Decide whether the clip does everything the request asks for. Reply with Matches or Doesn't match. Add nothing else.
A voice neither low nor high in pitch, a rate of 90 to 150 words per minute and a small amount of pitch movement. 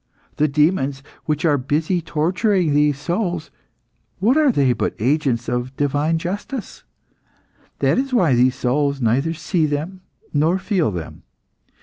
Doesn't match